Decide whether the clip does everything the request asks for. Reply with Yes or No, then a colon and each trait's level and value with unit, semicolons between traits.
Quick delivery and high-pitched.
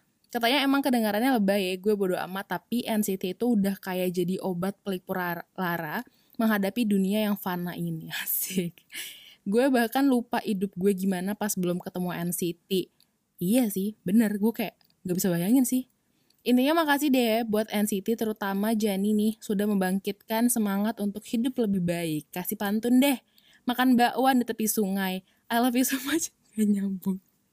Yes: fast, 160 wpm; high, 210 Hz